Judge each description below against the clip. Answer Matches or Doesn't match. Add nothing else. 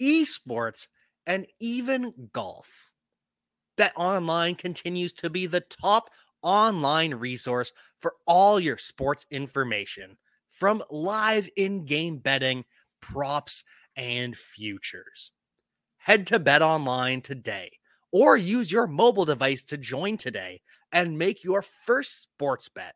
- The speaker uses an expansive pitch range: Matches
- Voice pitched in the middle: Matches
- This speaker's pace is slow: Matches